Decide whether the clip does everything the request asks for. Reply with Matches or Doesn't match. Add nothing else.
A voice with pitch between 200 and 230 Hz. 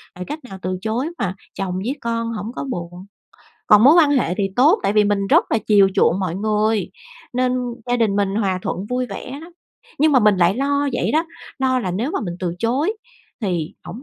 Matches